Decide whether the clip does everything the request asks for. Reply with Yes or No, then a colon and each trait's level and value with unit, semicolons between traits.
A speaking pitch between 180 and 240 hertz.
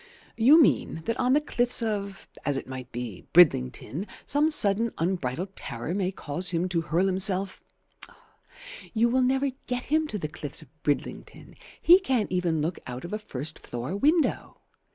Yes: high, 190 Hz